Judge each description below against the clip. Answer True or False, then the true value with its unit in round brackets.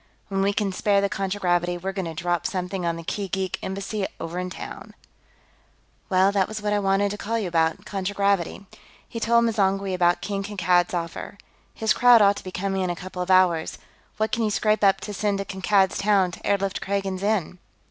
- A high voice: True (195 Hz)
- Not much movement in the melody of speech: True (1.9 semitones)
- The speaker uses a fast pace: True (210 wpm)